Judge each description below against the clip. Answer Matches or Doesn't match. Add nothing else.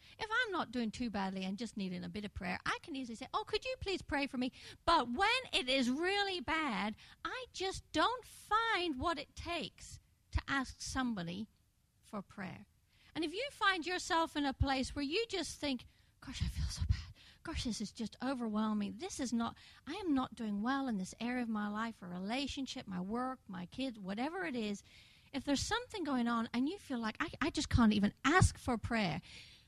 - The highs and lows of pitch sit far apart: Matches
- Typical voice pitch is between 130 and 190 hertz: Doesn't match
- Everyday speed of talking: Doesn't match